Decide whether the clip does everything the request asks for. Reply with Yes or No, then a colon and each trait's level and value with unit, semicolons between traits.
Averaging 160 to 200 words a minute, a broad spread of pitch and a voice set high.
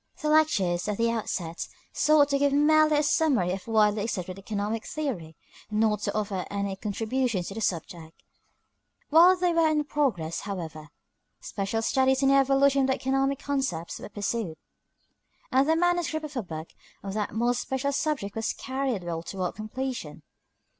Yes: average, 165 wpm; wide, 6.2 semitones; high, 230 Hz